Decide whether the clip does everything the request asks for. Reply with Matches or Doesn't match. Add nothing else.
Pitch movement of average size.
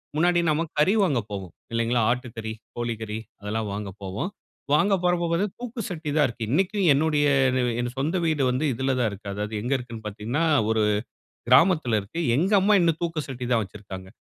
Doesn't match